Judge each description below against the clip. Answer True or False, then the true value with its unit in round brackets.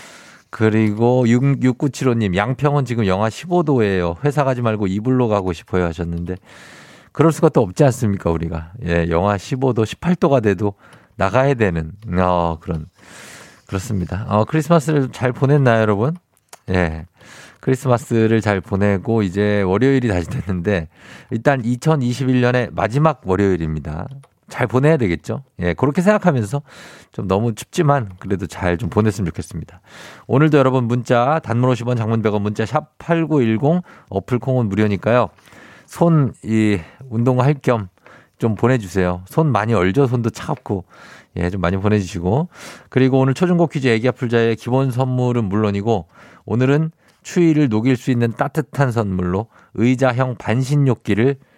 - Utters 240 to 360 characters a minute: True (305 characters per minute)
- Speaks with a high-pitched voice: False (115 Hz)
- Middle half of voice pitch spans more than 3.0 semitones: True (5.2 semitones)